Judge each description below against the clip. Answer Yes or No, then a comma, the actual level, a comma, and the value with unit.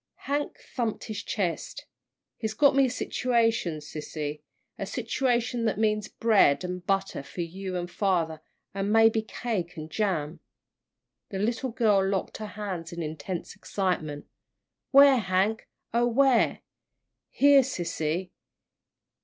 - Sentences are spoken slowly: Yes, slow, 130 wpm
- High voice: Yes, high, 200 Hz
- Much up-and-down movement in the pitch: No, average, 5.0 semitones